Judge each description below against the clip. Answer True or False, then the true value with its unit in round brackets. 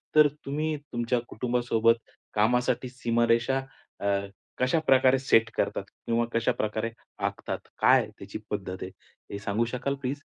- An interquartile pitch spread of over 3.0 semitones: False (2.6 semitones)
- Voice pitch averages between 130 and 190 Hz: False (120 Hz)